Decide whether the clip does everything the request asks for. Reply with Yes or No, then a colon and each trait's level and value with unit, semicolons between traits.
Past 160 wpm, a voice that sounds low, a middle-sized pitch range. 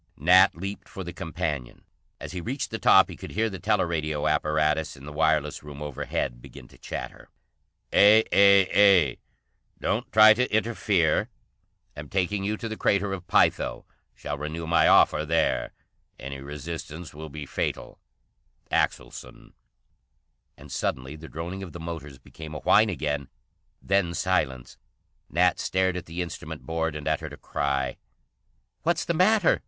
No: average, 155 wpm; very low, 85 Hz; average, 4.5 semitones